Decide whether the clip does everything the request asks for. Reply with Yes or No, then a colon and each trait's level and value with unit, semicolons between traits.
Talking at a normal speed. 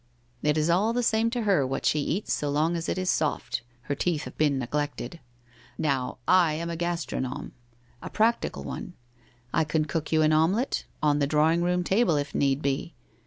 No: fast, 210 wpm